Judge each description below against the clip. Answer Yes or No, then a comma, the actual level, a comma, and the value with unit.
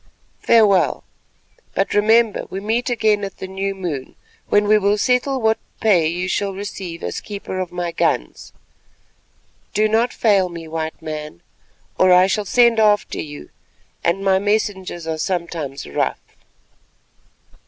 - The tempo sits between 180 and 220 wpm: No, average, 145 wpm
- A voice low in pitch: No, high, 195 Hz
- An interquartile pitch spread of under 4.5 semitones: Yes, average, 3.7 semitones